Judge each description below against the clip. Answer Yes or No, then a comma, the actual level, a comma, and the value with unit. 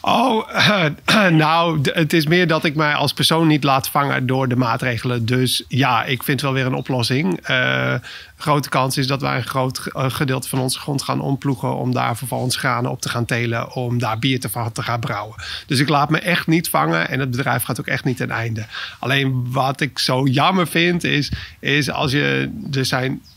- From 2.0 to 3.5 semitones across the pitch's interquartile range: Yes, average, 3.1 semitones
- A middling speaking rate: No, fast, 215 wpm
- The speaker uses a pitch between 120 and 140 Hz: Yes, low, 135 Hz